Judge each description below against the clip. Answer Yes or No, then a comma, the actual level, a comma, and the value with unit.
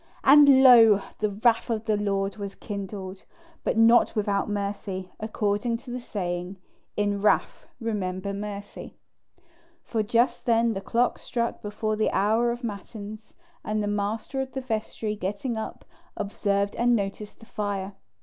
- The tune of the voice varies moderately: No, narrow, 2.3 semitones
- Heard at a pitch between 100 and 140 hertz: No, high, 210 Hz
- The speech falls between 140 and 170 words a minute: Yes, average, 150 wpm